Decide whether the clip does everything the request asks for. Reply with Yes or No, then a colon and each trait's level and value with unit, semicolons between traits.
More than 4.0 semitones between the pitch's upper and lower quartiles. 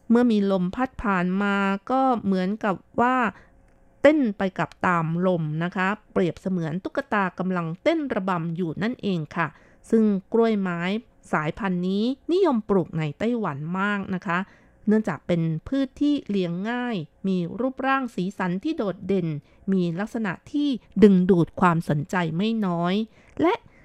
Yes: average, 4.5 semitones